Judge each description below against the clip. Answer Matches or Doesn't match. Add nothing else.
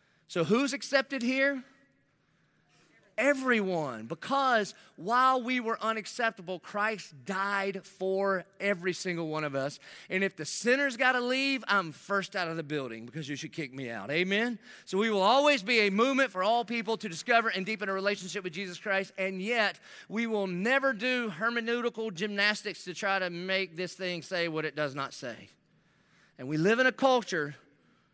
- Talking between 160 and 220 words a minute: Matches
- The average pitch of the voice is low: Doesn't match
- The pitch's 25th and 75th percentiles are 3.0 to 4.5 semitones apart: Doesn't match